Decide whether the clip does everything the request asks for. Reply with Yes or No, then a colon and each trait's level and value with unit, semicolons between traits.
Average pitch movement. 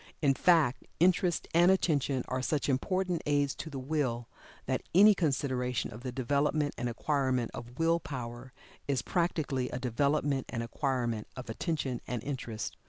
Yes: average, 3.9 semitones